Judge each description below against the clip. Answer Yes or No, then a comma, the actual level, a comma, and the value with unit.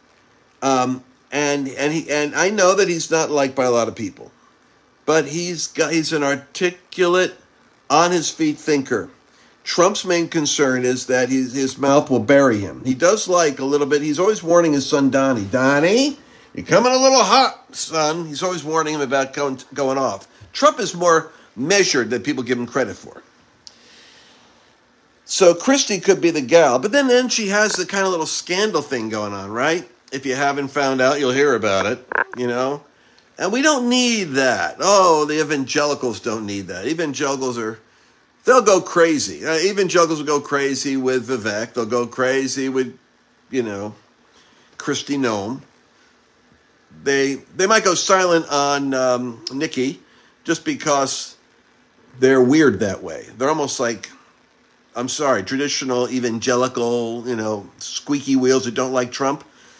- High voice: No, medium, 140 Hz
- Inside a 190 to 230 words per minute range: No, average, 160 wpm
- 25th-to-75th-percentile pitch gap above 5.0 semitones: No, average, 4.6 semitones